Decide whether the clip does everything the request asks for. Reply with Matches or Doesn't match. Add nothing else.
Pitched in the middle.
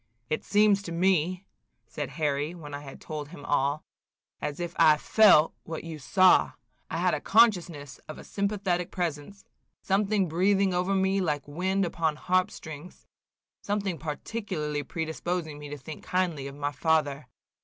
Matches